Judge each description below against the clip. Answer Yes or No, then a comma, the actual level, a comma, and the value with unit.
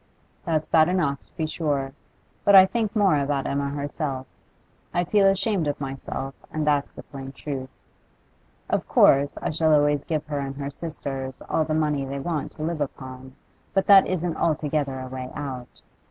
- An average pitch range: Yes, average, 3.1 semitones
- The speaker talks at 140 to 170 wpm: No, average, 180 wpm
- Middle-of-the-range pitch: Yes, medium, 145 Hz